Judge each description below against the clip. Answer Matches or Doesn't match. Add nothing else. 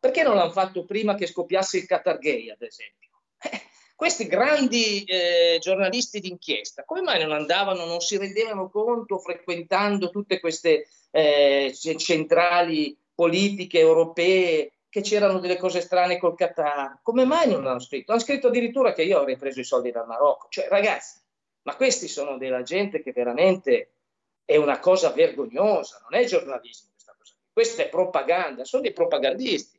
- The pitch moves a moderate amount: Doesn't match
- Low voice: Doesn't match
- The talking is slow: Doesn't match